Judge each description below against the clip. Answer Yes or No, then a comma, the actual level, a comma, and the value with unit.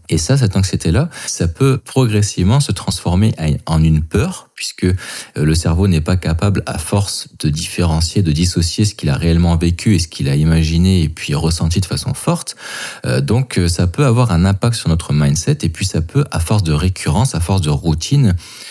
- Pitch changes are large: No, average, 4.7 semitones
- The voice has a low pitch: Yes, very low, 90 Hz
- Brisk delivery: No, average, 195 wpm